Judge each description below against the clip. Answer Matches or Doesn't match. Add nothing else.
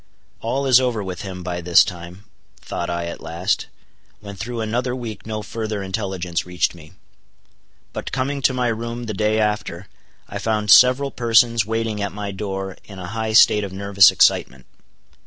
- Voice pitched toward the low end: Matches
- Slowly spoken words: Doesn't match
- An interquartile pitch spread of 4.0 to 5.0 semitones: Doesn't match